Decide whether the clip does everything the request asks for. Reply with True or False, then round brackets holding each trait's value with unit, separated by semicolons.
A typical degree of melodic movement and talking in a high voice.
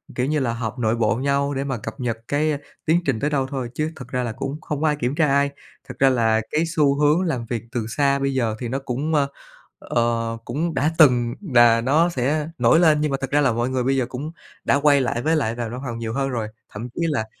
False (3.8 semitones; 135 Hz)